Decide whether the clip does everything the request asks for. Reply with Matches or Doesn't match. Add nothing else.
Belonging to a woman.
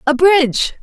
Matches